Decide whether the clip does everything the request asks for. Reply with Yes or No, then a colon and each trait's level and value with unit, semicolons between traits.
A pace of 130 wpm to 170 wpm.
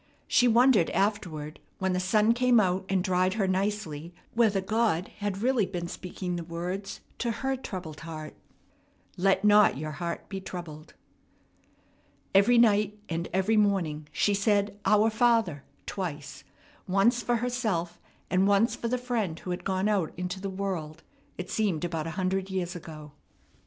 Yes: average, 155 wpm